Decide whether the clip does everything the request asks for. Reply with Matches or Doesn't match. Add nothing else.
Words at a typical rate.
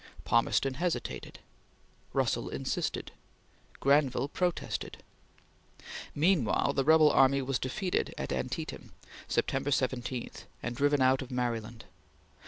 Doesn't match